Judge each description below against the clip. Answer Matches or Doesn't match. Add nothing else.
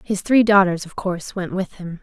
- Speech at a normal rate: Doesn't match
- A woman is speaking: Matches